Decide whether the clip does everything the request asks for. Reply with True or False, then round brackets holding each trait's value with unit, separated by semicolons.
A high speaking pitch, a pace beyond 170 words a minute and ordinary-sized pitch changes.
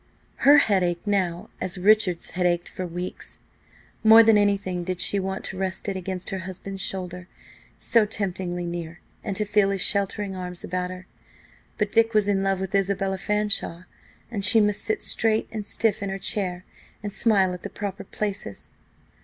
False (195 Hz; 180 wpm; 2.2 semitones)